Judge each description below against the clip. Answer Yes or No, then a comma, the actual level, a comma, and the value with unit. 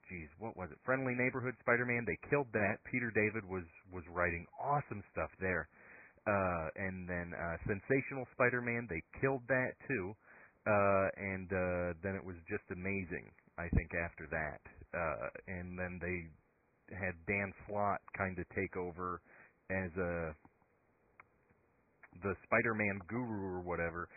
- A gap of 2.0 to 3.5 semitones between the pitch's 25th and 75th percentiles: No, average, 4.1 semitones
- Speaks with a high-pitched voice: No, very low, 95 Hz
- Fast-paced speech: No, average, 145 wpm